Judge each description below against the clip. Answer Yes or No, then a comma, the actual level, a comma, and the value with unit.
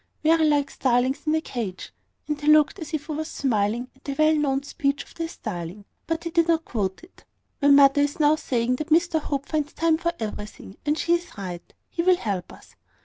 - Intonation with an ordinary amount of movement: Yes, average, 4.6 semitones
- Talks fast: Yes, fast, 220 wpm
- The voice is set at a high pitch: Yes, very high, 290 Hz